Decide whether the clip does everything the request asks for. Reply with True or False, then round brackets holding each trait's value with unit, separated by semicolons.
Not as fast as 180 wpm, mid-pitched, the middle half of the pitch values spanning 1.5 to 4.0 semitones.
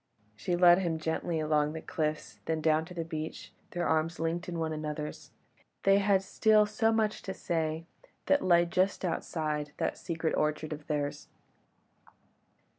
True (160 wpm; 165 Hz; 2.6 semitones)